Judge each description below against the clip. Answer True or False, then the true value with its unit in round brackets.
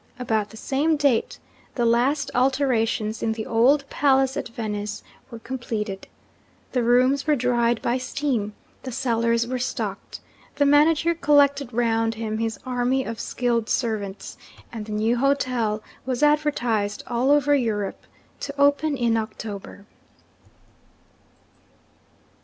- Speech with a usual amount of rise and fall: True (3.6 semitones)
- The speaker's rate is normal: False (130 wpm)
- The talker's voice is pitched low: False (240 Hz)